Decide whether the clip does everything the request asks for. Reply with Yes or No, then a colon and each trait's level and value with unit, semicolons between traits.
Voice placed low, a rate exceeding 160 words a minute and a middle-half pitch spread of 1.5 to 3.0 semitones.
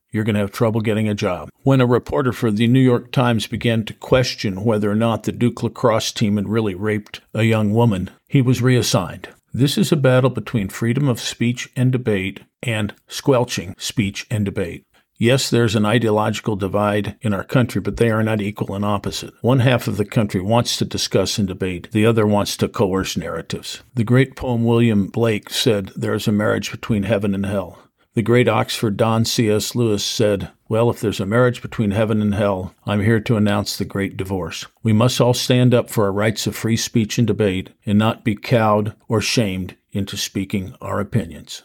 Yes: low, 110 Hz; fast, 205 wpm; narrow, 2.5 semitones